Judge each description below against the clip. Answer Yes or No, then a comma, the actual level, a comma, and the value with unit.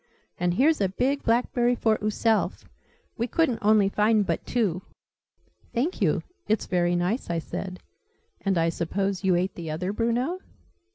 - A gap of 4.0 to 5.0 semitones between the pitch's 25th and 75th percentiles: Yes, average, 4.7 semitones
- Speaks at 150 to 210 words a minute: Yes, average, 155 wpm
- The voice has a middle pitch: No, high, 210 Hz